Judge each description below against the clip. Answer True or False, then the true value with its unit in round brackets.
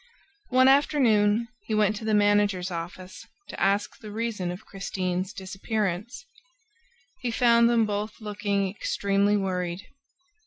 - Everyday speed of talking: False (125 wpm)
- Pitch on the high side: True (205 Hz)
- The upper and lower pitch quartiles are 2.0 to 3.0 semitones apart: True (2.6 semitones)